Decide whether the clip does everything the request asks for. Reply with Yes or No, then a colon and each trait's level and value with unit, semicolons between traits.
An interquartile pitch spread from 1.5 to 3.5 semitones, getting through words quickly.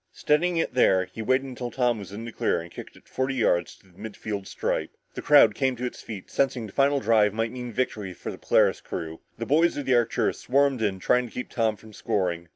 No: average, 4.2 semitones; fast, 245 wpm